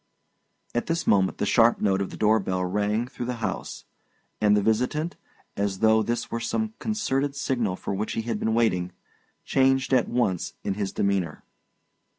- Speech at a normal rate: Yes, average, 175 wpm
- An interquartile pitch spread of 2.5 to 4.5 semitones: Yes, average, 4.0 semitones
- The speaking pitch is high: No, low, 110 Hz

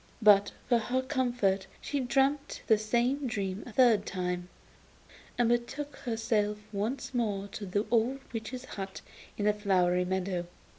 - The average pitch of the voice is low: No, high, 220 Hz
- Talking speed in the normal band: Yes, average, 145 wpm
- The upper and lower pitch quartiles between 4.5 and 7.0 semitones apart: No, average, 3.9 semitones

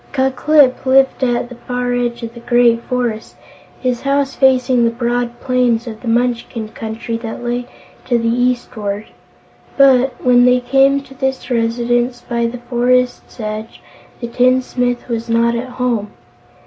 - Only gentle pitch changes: Yes, narrow, 1.3 semitones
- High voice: Yes, high, 245 Hz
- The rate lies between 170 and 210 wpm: No, average, 155 wpm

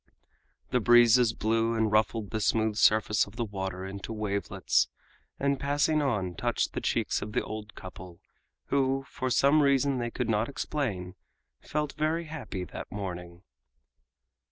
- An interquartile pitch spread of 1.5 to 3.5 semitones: No, average, 5.1 semitones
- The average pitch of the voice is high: No, low, 110 Hz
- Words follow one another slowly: No, average, 150 wpm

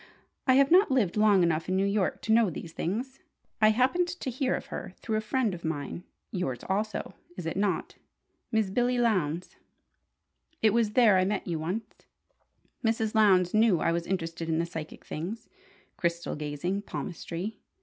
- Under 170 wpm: No, average, 175 wpm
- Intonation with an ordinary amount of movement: Yes, average, 4.7 semitones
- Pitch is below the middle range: No, high, 200 Hz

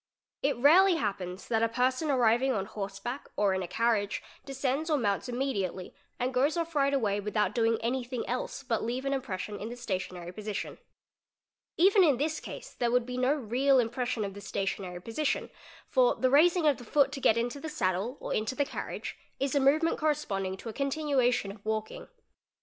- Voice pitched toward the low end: No, high, 245 Hz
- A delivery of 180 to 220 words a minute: Yes, average, 195 wpm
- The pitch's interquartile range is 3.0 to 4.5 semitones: No, average, 4.9 semitones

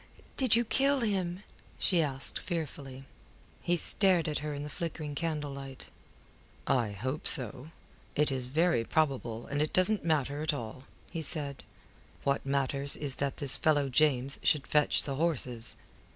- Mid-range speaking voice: Yes, medium, 145 Hz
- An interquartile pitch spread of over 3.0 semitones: Yes, average, 3.4 semitones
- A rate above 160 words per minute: No, average, 150 wpm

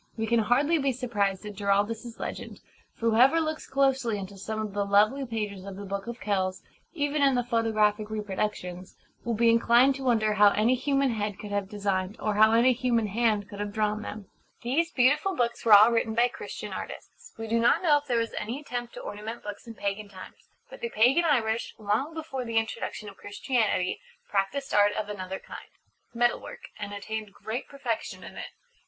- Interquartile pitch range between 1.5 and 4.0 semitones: Yes, average, 3.2 semitones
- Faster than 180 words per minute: Yes, average, 200 wpm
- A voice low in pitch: No, high, 225 Hz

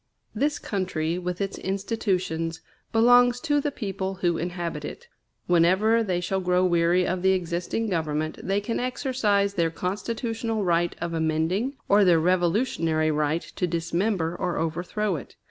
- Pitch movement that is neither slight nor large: Yes, average, 4.0 semitones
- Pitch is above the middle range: No, medium, 180 Hz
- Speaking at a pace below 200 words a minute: Yes, average, 145 wpm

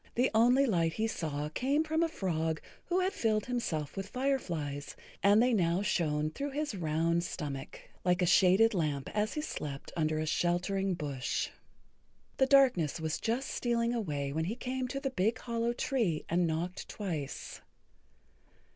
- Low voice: No, high, 190 Hz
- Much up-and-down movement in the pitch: Yes, wide, 7.3 semitones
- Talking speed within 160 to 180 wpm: Yes, average, 165 wpm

